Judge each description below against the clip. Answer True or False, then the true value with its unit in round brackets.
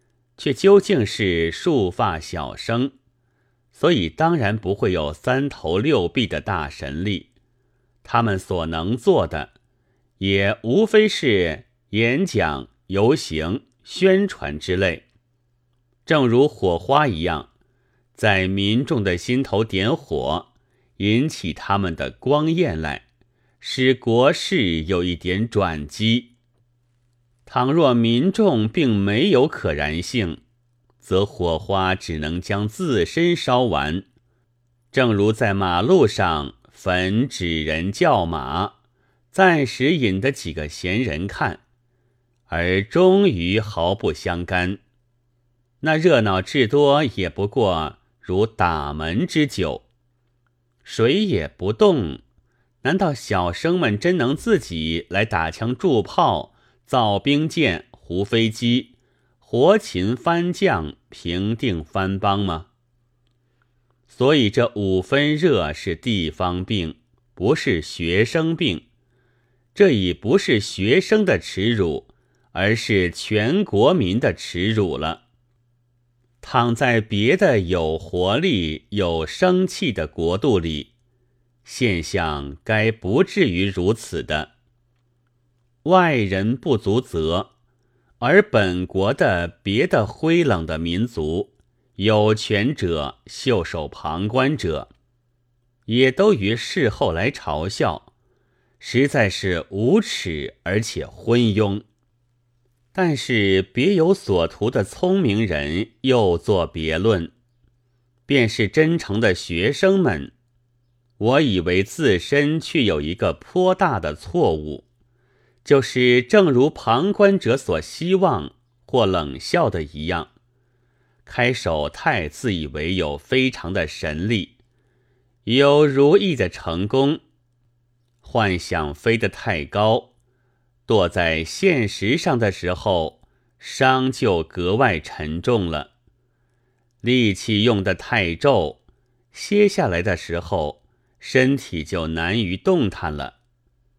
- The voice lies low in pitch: True (120 Hz)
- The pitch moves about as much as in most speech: True (4.8 semitones)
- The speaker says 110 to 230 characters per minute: True (155 characters per minute)